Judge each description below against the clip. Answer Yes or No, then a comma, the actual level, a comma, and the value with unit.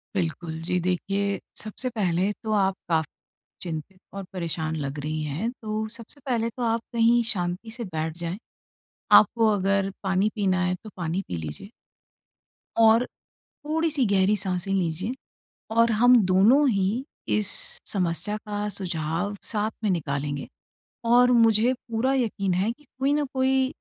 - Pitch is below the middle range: No, high, 200 Hz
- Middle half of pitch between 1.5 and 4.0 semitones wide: No, average, 4.6 semitones